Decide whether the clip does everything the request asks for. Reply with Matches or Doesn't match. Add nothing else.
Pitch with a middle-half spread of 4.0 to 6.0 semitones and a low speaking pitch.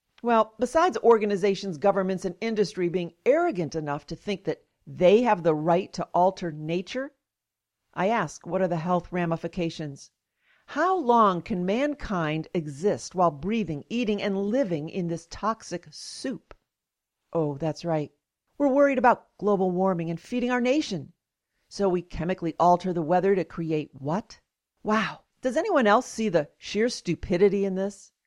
Doesn't match